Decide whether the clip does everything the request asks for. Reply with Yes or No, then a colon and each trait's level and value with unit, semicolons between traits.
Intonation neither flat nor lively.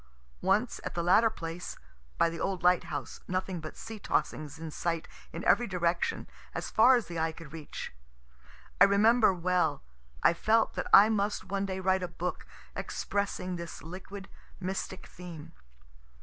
Yes: average, 3.0 semitones